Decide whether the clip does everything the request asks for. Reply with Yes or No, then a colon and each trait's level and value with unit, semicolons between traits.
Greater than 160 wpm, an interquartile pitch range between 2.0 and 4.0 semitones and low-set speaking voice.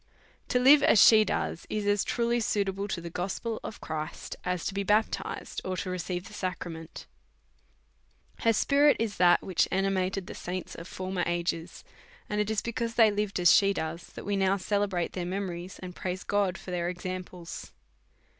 No: average, 180 wpm; average, 2.7 semitones; high, 190 Hz